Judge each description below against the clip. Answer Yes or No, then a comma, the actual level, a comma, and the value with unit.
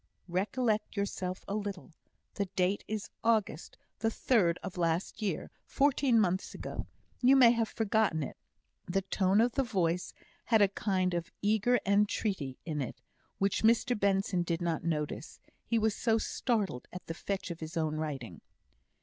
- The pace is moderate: Yes, average, 160 wpm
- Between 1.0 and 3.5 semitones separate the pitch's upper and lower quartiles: No, average, 4.3 semitones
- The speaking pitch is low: No, high, 195 Hz